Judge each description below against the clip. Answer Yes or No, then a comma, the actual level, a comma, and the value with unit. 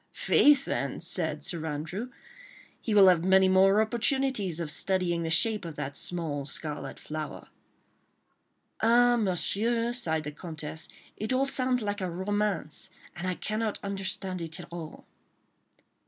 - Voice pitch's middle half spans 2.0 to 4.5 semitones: No, average, 5.1 semitones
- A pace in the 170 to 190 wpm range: No, average, 140 wpm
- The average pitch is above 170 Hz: Yes, high, 190 Hz